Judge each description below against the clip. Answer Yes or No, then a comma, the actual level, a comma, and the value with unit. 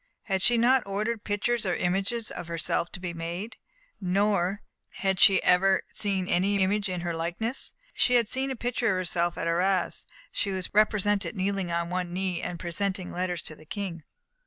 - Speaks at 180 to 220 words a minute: Yes, average, 185 wpm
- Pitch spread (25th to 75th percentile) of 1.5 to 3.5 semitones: Yes, average, 2.8 semitones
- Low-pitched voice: No, high, 190 Hz